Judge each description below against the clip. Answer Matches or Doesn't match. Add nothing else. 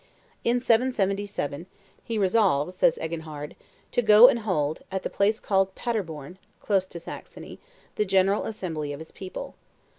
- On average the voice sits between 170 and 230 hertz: Matches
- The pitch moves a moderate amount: Matches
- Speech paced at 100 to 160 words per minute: Matches